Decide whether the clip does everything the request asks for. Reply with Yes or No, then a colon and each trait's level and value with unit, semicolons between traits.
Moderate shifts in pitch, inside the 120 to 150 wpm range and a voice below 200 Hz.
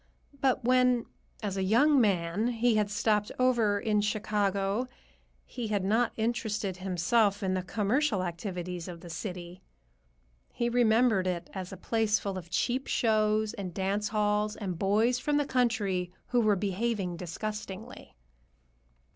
No: average, 3.6 semitones; average, 145 wpm; high, 210 Hz